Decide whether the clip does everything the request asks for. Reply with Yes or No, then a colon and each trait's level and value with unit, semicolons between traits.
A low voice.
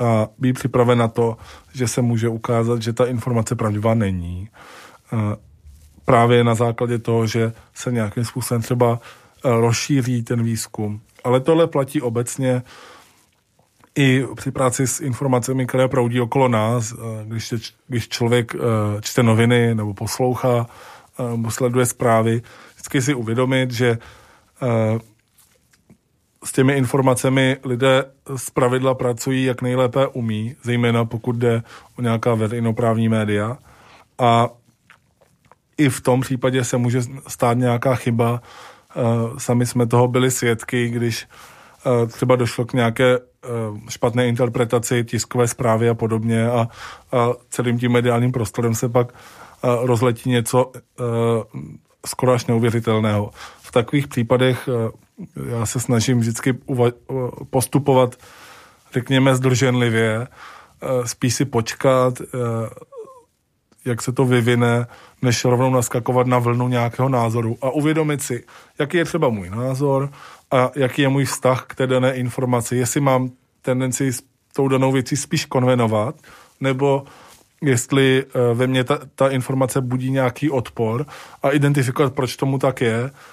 Yes: low, 125 Hz